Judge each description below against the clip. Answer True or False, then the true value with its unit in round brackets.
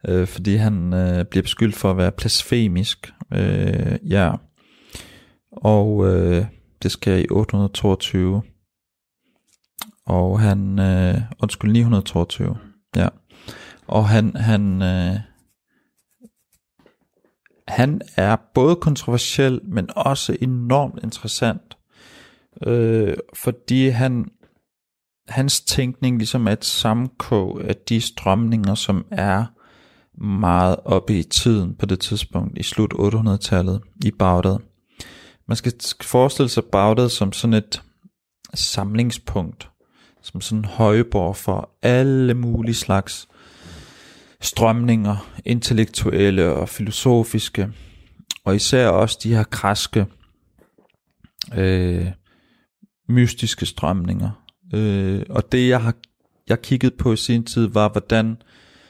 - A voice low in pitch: True (105 Hz)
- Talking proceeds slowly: True (105 wpm)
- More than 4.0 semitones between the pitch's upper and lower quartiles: False (3.5 semitones)